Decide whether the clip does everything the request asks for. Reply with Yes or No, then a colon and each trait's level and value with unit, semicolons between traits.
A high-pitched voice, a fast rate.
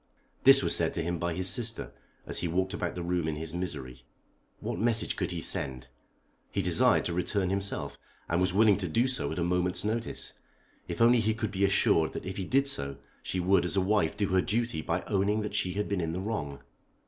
No: very low, 90 Hz; fast, 230 wpm